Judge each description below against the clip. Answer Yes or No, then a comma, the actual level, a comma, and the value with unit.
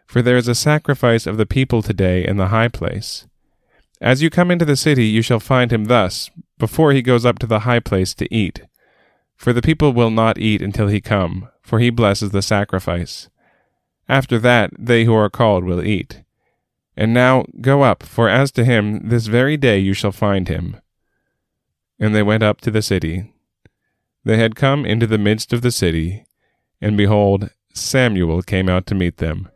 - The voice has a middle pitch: No, low, 110 Hz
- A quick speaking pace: No, average, 195 wpm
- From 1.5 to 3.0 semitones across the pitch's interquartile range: No, average, 3.7 semitones